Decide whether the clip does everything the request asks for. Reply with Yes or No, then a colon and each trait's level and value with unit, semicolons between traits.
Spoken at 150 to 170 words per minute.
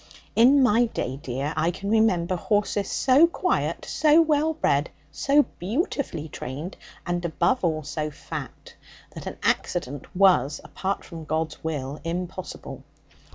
No: slow, 135 wpm